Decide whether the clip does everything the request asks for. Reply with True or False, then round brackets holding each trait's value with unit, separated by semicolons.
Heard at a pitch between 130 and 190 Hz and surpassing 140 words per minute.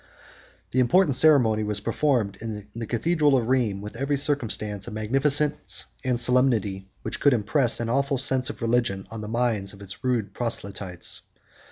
False (120 Hz; 165 wpm)